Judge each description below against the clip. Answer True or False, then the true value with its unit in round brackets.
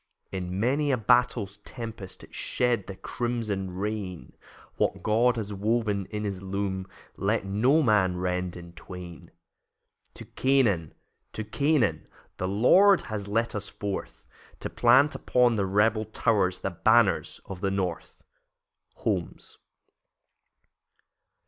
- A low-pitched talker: True (105 Hz)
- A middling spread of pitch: True (3.8 semitones)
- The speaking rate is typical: False (125 wpm)